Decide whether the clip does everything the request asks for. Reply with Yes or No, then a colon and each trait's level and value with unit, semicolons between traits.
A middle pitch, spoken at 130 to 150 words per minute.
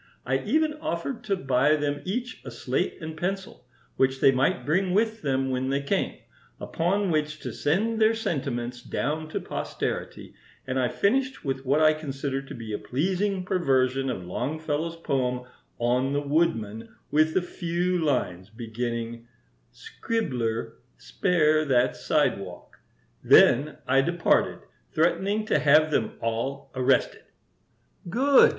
Yes: medium, 145 Hz; average, 140 wpm